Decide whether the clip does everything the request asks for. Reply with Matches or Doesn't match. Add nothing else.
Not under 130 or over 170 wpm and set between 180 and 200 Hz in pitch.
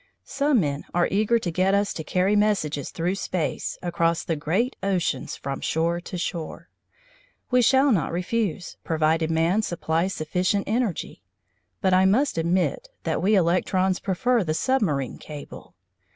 Matches